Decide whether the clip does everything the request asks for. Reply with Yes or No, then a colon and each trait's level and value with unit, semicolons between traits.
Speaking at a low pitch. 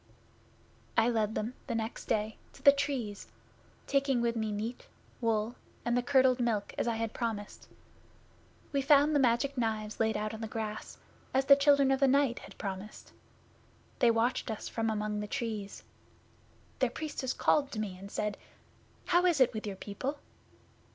No: high, 230 Hz